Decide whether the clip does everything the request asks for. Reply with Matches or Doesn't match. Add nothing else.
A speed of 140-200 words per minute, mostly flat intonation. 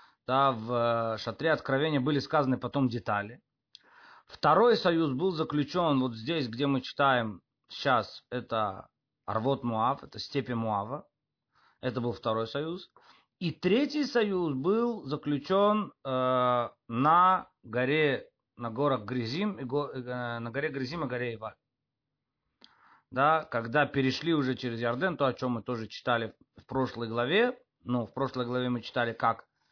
Doesn't match